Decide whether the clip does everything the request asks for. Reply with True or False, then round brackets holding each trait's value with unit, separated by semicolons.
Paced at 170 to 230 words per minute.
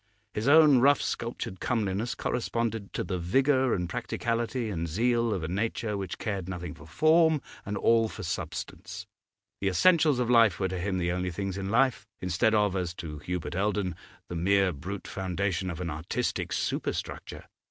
True (175 wpm)